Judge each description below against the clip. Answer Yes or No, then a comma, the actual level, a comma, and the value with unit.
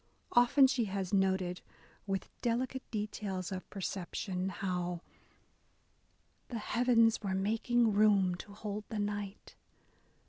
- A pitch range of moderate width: Yes, average, 3.1 semitones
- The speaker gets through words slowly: Yes, slow, 110 wpm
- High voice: Yes, high, 205 Hz